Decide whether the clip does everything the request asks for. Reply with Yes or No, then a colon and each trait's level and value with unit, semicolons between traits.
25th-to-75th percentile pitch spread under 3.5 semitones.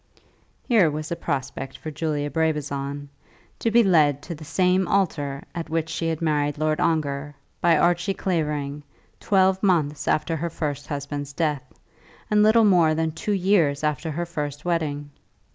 Yes: average, 3.0 semitones